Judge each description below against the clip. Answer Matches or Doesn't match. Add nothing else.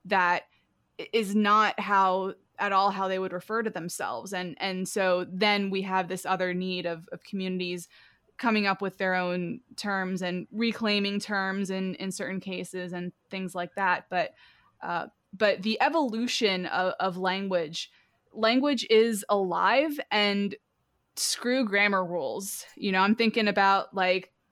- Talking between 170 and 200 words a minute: Doesn't match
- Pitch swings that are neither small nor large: Doesn't match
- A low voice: Doesn't match